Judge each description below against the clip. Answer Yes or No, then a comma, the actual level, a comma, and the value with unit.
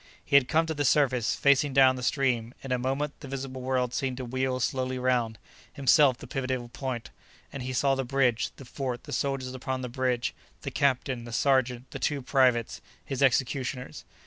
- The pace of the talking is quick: No, average, 195 wpm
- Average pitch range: No, narrow, 1.5 semitones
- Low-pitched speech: Yes, low, 130 Hz